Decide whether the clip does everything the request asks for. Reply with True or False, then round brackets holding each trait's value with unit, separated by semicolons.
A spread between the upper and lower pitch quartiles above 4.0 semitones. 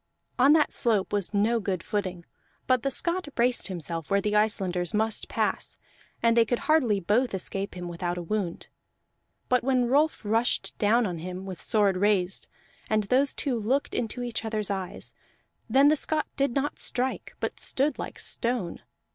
True (4.7 semitones)